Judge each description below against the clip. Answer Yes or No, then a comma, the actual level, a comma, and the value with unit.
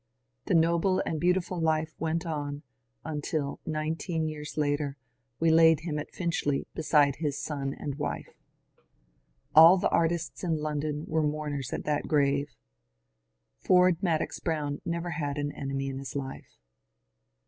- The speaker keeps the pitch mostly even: Yes, narrow, 2.2 semitones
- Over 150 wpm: No, average, 145 wpm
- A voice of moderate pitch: Yes, medium, 155 Hz